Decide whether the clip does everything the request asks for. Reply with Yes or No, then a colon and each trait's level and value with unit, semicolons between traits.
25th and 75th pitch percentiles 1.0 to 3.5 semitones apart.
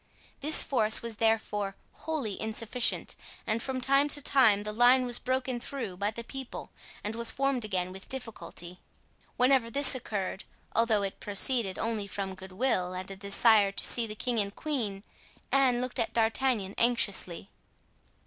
No: average, 4.2 semitones